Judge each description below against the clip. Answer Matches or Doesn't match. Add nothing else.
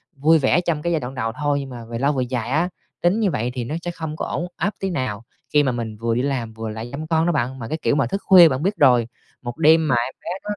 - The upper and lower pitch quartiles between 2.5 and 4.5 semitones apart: Doesn't match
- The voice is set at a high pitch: Doesn't match